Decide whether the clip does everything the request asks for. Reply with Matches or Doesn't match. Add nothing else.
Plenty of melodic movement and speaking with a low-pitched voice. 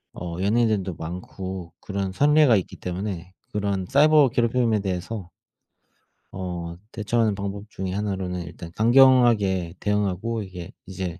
Doesn't match